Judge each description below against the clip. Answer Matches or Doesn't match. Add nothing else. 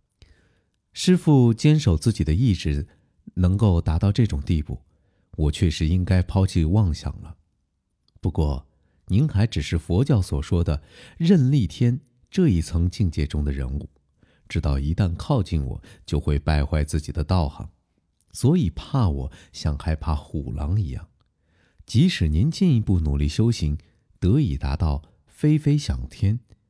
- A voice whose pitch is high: Doesn't match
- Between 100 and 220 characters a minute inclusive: Matches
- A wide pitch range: Matches